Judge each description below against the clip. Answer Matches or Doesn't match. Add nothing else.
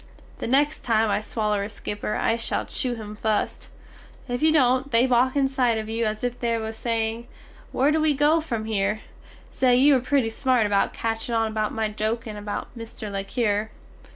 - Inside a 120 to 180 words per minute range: Doesn't match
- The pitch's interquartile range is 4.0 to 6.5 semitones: Doesn't match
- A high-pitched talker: Matches